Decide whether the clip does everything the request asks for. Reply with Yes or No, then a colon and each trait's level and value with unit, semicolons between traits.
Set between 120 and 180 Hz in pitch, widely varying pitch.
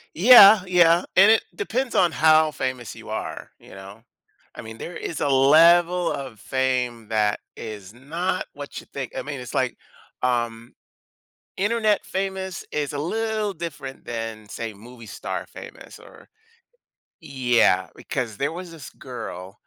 Yes: medium, 140 Hz; wide, 7.3 semitones